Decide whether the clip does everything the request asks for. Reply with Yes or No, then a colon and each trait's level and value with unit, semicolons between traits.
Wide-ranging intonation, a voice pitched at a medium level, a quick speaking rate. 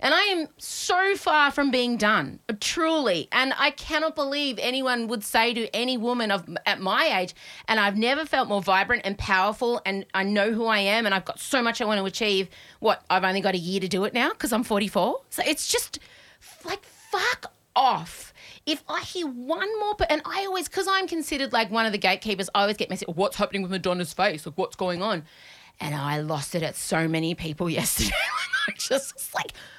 No: wide, 7.3 semitones; high, 220 Hz; fast, 215 wpm